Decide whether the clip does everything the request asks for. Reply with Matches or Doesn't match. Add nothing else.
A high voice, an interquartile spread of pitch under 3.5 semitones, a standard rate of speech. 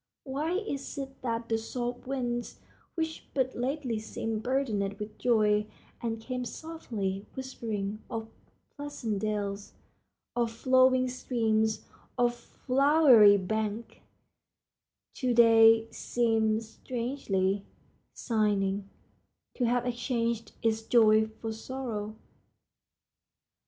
Doesn't match